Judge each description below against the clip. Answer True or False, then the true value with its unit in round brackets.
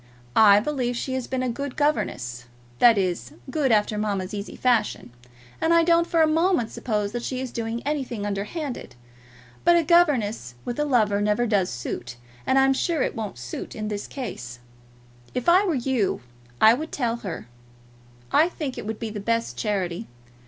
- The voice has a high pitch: True (235 Hz)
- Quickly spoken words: False (180 wpm)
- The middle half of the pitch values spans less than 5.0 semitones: False (5.5 semitones)